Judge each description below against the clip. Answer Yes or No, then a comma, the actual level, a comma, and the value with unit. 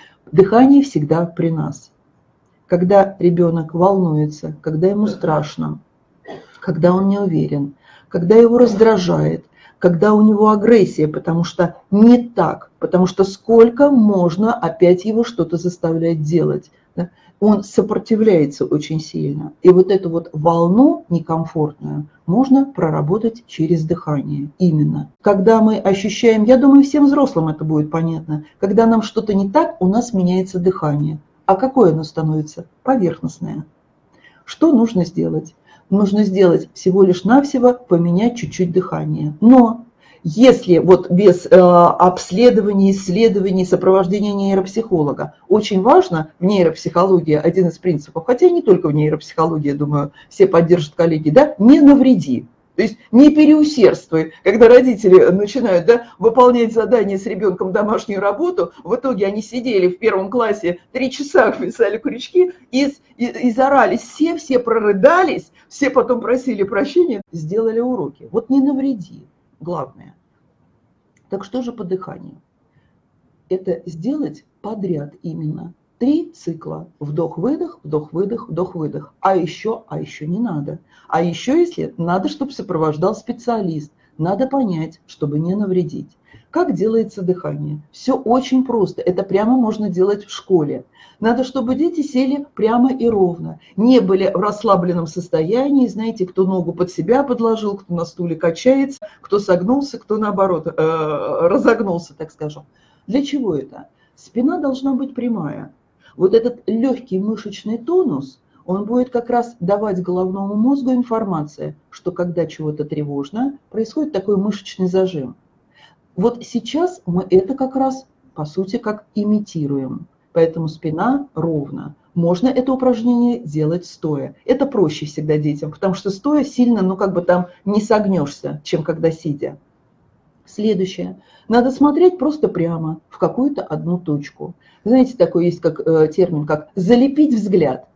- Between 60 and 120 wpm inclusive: No, average, 135 wpm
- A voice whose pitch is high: Yes, high, 195 Hz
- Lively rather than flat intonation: Yes, wide, 6.1 semitones